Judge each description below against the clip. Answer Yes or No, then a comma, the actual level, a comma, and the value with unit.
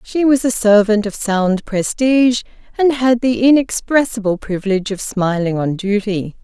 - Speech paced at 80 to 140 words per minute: No, average, 150 wpm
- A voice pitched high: Yes, high, 220 Hz